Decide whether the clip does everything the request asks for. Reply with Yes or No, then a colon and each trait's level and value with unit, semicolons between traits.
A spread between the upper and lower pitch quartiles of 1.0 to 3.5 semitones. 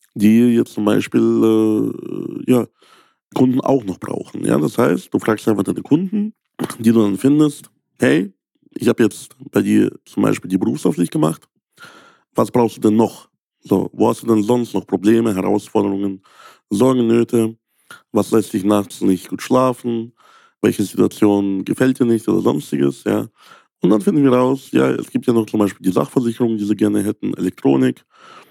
Yes: average, 3.1 semitones